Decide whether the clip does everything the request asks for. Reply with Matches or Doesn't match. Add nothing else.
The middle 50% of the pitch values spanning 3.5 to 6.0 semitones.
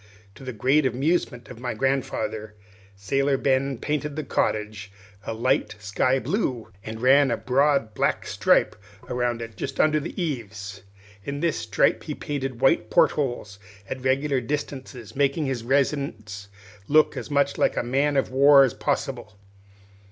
Matches